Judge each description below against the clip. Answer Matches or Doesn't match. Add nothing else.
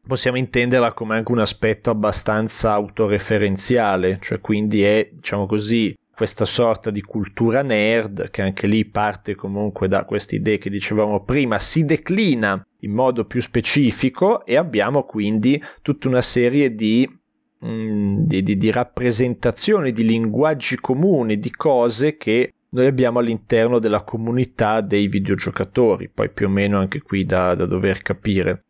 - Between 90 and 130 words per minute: Doesn't match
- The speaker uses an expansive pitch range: Doesn't match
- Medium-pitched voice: Doesn't match